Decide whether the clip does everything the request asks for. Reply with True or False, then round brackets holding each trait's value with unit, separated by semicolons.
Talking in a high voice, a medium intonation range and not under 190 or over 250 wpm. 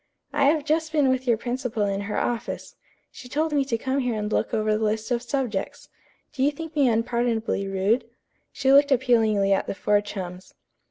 True (240 Hz; 4.3 semitones; 200 wpm)